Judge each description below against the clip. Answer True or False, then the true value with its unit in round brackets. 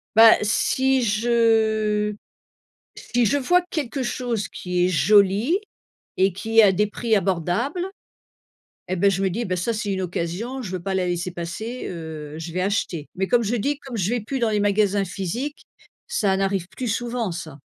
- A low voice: False (210 Hz)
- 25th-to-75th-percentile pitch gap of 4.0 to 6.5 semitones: True (4.4 semitones)